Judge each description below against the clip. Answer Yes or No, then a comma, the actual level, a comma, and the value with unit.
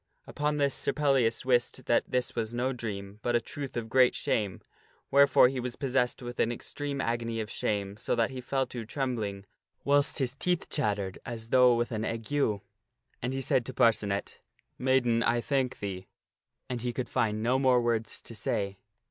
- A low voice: Yes, low, 120 Hz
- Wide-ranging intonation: No, average, 2.9 semitones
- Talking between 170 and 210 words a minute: Yes, average, 190 wpm